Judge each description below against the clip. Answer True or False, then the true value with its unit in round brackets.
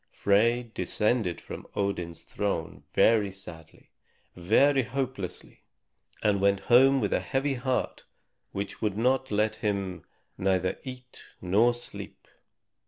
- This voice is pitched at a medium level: False (105 Hz)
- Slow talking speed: True (110 wpm)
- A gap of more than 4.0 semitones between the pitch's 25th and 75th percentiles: True (4.4 semitones)